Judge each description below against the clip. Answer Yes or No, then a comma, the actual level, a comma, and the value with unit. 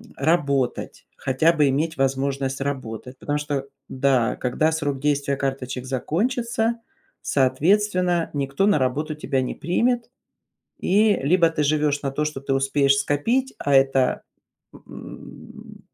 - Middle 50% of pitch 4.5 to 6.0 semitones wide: No, average, 3.5 semitones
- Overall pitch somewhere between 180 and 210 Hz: No, medium, 145 Hz